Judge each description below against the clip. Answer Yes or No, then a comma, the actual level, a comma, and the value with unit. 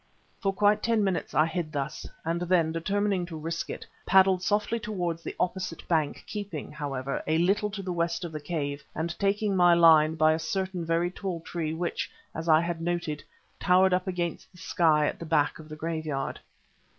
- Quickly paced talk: No, average, 195 wpm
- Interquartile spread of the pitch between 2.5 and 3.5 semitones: Yes, average, 2.9 semitones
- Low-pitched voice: No, medium, 170 Hz